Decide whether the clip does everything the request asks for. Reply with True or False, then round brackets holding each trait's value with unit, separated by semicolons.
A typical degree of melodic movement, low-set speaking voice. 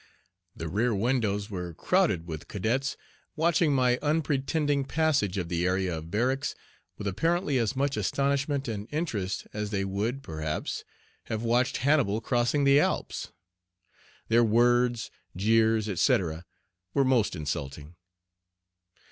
False (6.0 semitones; 115 Hz)